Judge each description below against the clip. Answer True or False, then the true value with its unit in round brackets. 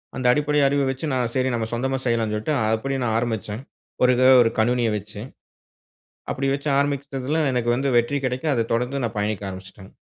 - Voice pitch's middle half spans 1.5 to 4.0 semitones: True (3.4 semitones)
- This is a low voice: True (125 Hz)